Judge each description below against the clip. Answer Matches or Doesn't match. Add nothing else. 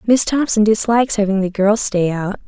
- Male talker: Doesn't match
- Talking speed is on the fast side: Doesn't match